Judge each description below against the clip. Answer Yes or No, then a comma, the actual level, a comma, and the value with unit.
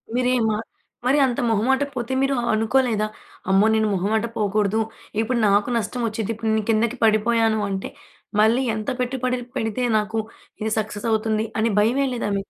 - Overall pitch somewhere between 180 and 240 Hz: Yes, high, 225 Hz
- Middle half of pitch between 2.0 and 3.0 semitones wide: Yes, narrow, 2.5 semitones